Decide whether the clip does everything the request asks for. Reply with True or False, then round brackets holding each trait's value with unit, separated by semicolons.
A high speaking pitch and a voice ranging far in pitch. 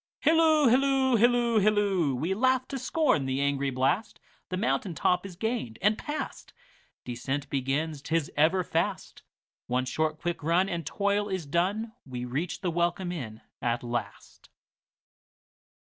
False (175 Hz; 7.6 semitones)